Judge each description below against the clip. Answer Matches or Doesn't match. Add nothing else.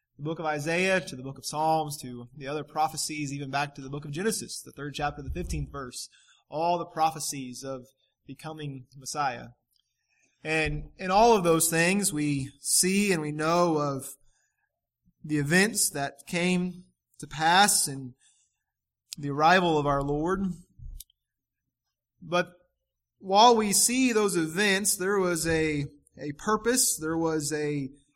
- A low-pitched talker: Doesn't match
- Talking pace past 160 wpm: Doesn't match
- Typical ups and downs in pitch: Matches